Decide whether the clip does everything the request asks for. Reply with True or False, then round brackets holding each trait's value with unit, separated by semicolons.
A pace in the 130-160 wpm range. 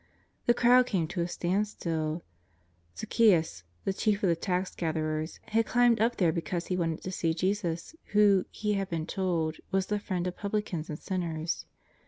False (180 wpm)